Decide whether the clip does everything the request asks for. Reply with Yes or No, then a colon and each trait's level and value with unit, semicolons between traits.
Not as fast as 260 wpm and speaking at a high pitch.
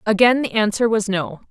Yes: average, 200 wpm; high, 215 Hz